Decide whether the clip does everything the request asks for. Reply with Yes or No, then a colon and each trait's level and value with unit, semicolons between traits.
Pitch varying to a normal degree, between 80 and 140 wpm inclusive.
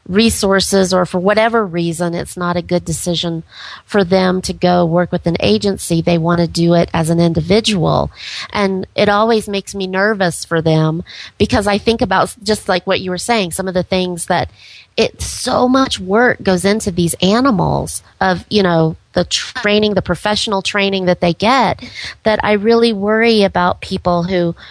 No: average, 3.1 semitones; average, 180 wpm